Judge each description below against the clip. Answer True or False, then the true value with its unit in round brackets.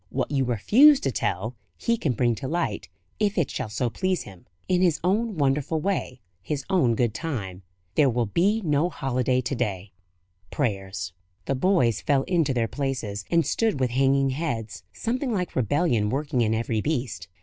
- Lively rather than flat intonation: True (6.8 semitones)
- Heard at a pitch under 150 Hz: True (135 Hz)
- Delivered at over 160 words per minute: True (175 wpm)